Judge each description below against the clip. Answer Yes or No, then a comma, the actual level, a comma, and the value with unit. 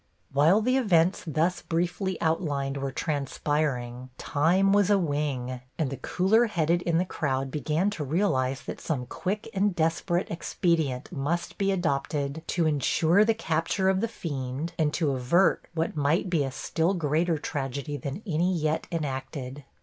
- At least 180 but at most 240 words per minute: No, average, 155 wpm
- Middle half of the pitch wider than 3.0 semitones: Yes, average, 4.3 semitones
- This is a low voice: No, medium, 160 Hz